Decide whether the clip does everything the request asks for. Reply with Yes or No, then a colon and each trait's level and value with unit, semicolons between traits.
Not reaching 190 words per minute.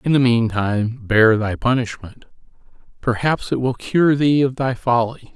Yes: average, 155 wpm